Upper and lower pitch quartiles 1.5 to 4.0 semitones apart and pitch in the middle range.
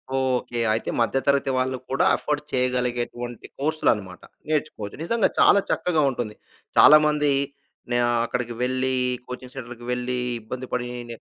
No: narrow, 2.5 semitones; low, 125 Hz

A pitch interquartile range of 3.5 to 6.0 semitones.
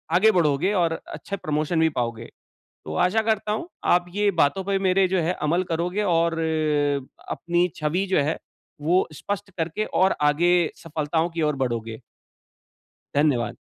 Yes: average, 4.1 semitones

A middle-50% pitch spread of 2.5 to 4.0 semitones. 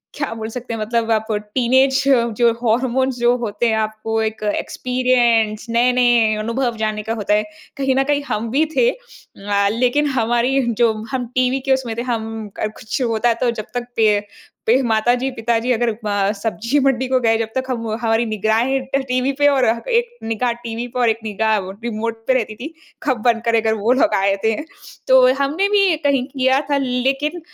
Yes: average, 2.9 semitones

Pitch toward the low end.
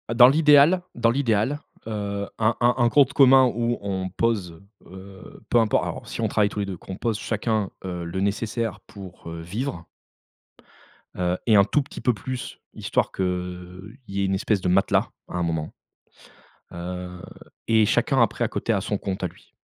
Yes: low, 105 Hz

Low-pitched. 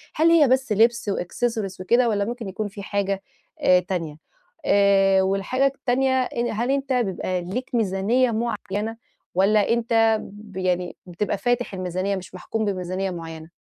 No: high, 205 Hz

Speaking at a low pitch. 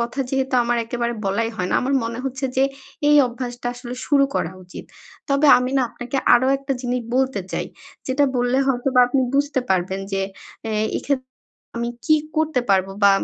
No: very high, 250 Hz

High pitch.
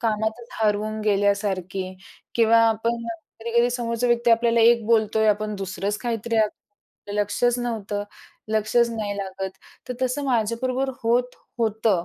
Yes: high, 225 Hz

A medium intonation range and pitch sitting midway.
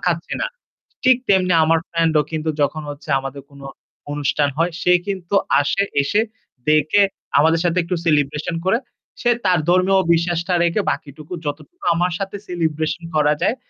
Yes: average, 3.2 semitones; medium, 165 Hz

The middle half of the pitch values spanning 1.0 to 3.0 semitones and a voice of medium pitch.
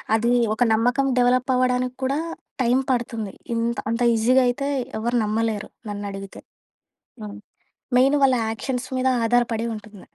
No: narrow, 2.5 semitones; high, 240 Hz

